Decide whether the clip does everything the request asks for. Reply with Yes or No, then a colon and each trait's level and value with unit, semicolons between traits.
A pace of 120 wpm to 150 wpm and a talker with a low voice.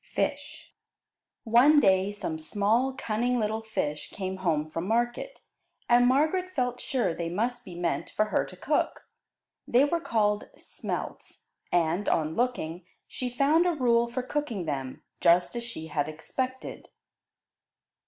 No: average, 145 wpm; high, 225 Hz